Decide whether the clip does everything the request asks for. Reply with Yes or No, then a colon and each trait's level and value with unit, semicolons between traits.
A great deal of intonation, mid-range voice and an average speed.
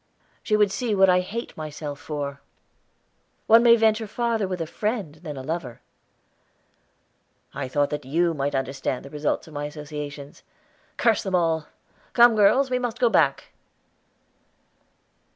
Yes: wide, 7.0 semitones; medium, 165 Hz; average, 150 wpm